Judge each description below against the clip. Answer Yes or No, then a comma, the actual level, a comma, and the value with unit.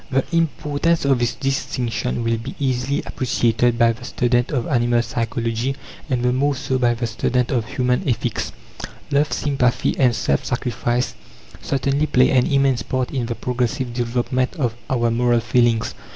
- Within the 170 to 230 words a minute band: No, average, 160 wpm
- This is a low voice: Yes, low, 125 Hz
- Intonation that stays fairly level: Yes, narrow, 2.2 semitones